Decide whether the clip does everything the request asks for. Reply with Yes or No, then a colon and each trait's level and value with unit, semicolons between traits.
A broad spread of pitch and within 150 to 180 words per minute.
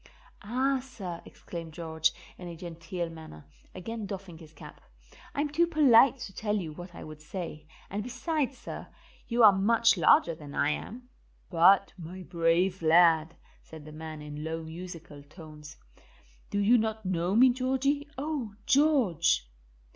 Yes: wide, 6.4 semitones; average, 155 wpm